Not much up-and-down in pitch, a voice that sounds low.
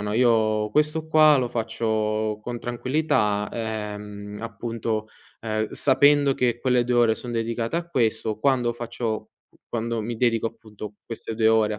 Yes: narrow, 2.2 semitones; low, 115 Hz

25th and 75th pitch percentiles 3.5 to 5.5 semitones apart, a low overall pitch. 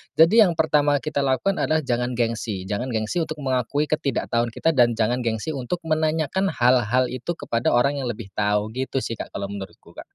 Yes: average, 5.0 semitones; low, 130 Hz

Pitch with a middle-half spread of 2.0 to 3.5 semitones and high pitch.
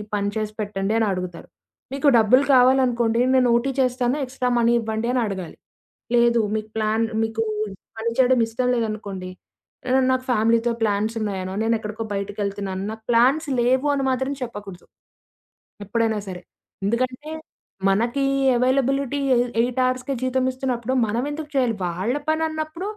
Yes: average, 3.2 semitones; high, 235 Hz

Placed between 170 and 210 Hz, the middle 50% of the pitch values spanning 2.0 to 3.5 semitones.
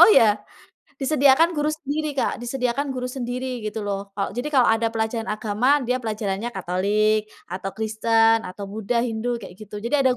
No: high, 225 Hz; average, 3.0 semitones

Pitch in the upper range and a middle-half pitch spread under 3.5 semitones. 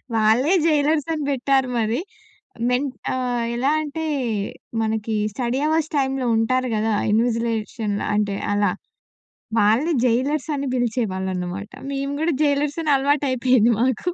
No: very high, 250 Hz; average, 4.2 semitones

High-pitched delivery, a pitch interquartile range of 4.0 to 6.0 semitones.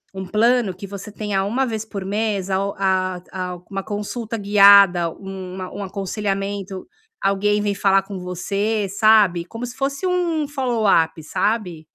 No: high, 200 Hz; narrow, 2.4 semitones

